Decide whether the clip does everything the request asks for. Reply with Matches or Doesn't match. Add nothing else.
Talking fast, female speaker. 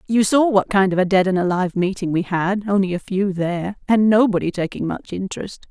Matches